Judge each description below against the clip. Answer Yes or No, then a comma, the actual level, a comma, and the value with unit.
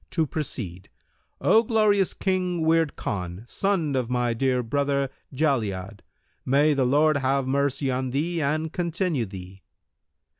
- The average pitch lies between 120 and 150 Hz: Yes, medium, 140 Hz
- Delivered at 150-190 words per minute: No, slow, 135 wpm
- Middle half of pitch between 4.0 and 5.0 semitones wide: Yes, average, 4.6 semitones